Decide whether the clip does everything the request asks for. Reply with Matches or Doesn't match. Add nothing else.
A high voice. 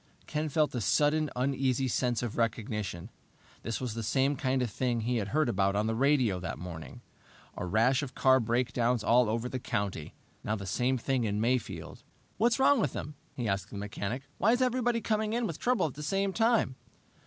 Doesn't match